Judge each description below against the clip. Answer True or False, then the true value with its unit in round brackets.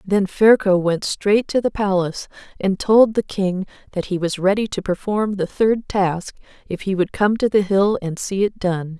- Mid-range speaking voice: False (195 Hz)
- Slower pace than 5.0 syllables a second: True (4.5 syllables/s)